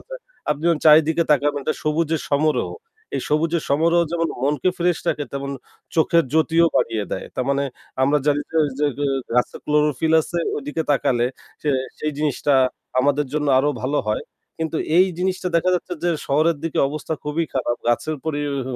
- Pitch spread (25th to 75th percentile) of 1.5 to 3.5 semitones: Yes, narrow, 2.4 semitones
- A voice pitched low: No, medium, 150 Hz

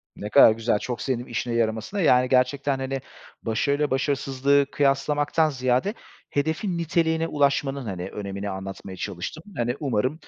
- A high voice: No, low, 130 Hz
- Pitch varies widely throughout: No, average, 4.2 semitones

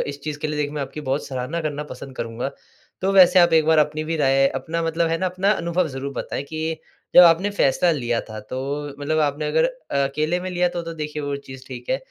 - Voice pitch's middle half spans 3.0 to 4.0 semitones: Yes, average, 3.4 semitones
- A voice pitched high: No, medium, 155 Hz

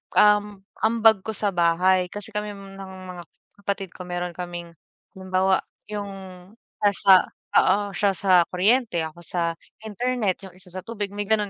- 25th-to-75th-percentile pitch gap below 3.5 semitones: Yes, narrow, 2.4 semitones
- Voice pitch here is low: No, high, 195 Hz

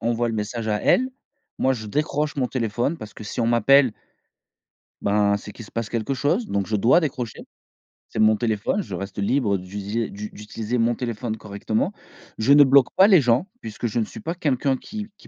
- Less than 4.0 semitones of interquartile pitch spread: No, average, 4.5 semitones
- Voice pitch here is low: Yes, low, 115 Hz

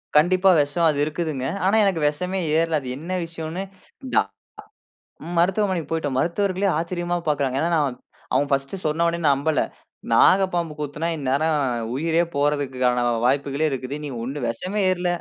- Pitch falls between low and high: Yes, medium, 160 Hz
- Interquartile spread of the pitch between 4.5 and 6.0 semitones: No, average, 3.6 semitones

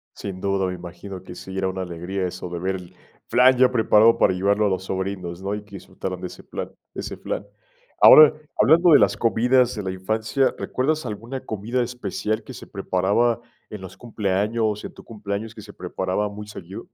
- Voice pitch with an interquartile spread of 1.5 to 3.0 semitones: No, average, 3.5 semitones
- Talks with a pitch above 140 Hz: No, low, 100 Hz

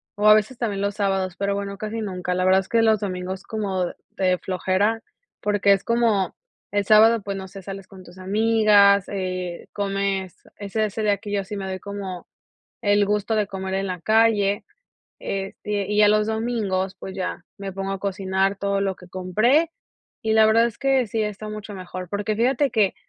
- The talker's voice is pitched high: Yes, high, 200 Hz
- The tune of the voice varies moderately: No, narrow, 2.0 semitones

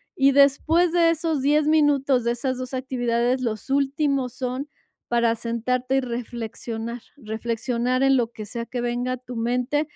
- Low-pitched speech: No, very high, 255 Hz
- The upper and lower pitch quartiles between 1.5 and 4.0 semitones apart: Yes, narrow, 2.6 semitones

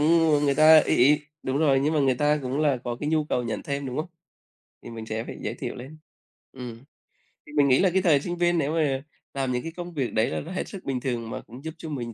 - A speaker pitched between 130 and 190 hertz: Yes, medium, 140 Hz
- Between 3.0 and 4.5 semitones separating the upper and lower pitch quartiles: Yes, average, 3.6 semitones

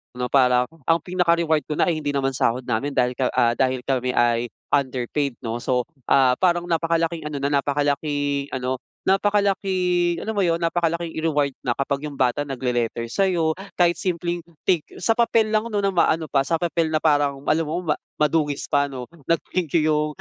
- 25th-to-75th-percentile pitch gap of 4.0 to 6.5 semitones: Yes, average, 4.3 semitones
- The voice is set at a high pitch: No, medium, 150 Hz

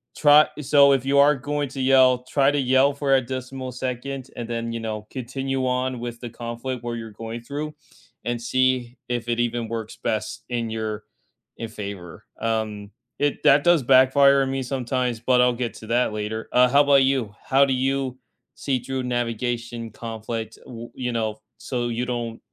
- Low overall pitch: Yes, low, 125 Hz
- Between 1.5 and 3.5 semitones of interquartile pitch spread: Yes, narrow, 2.5 semitones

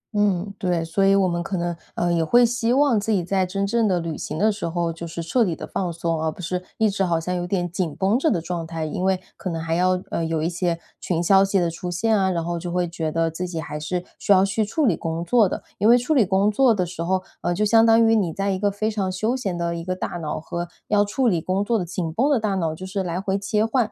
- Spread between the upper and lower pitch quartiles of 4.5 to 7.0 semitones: No, average, 3.4 semitones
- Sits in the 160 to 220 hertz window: Yes, medium, 185 Hz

